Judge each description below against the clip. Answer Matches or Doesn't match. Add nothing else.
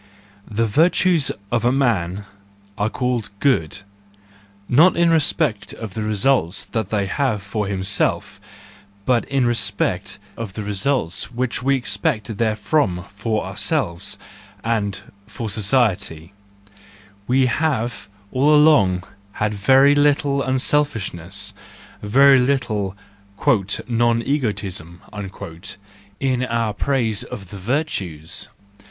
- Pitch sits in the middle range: Doesn't match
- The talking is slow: Matches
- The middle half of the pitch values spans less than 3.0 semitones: Doesn't match